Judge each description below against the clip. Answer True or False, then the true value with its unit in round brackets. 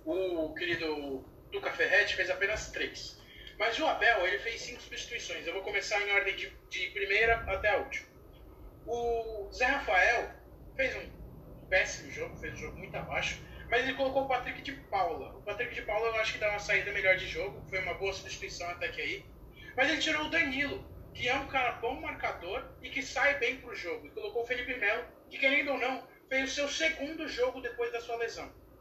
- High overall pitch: True (235 Hz)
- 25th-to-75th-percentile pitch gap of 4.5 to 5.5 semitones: True (5.1 semitones)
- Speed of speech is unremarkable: False (205 wpm)